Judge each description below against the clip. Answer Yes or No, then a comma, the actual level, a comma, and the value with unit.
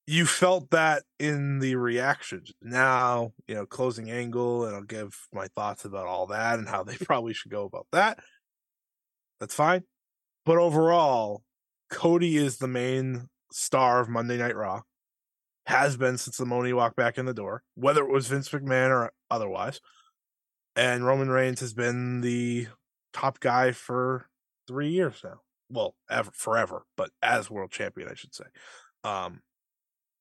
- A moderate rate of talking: Yes, average, 160 wpm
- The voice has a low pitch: Yes, low, 130 Hz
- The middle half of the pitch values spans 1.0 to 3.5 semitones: Yes, average, 2.8 semitones